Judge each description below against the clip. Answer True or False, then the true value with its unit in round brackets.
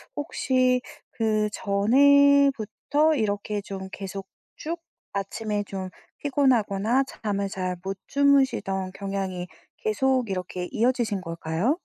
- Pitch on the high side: True (215 Hz)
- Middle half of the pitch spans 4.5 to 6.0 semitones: True (5.5 semitones)